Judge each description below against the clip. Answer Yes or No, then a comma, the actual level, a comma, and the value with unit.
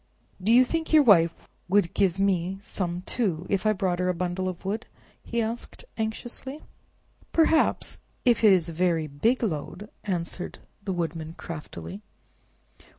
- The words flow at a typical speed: Yes, average, 150 wpm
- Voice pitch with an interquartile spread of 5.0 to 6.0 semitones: No, average, 4.5 semitones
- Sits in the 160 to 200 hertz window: Yes, high, 190 Hz